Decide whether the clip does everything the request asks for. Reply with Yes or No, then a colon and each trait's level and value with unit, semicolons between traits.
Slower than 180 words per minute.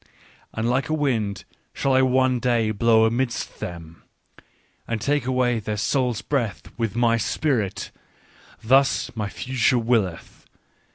Yes: average, 145 wpm